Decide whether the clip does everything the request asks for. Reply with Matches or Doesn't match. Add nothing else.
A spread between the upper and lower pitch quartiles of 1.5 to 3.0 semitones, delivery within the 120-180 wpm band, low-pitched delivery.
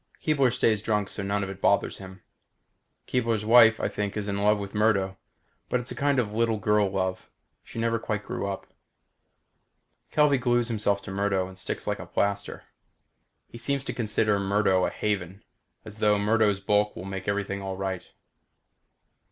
Matches